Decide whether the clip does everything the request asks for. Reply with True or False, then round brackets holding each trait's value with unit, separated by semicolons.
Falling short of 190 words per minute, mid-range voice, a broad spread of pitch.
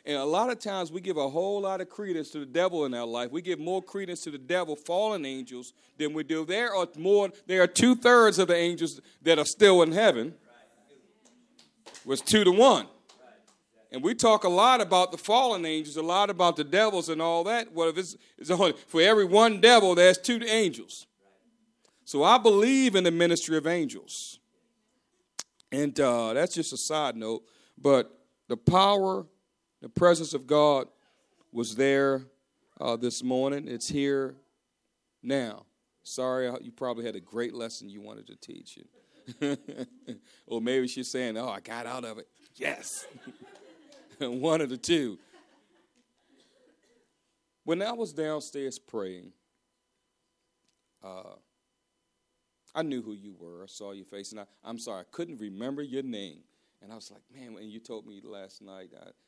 True (170 wpm; 155 Hz; 7.0 semitones)